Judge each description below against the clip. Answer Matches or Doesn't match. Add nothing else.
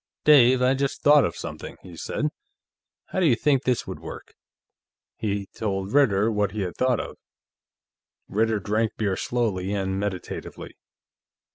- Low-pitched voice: Matches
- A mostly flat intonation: Doesn't match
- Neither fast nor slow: Matches